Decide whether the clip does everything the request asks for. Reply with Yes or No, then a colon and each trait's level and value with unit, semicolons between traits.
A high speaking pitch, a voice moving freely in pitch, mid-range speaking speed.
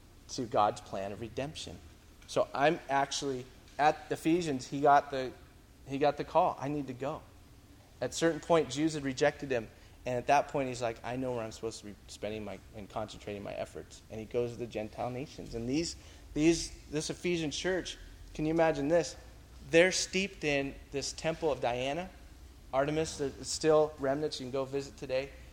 No: low, 135 Hz; wide, 6.3 semitones; average, 190 wpm